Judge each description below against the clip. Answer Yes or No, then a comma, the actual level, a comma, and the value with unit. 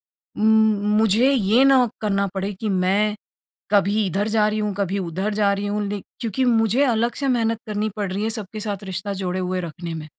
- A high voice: Yes, high, 205 Hz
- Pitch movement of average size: No, narrow, 2.3 semitones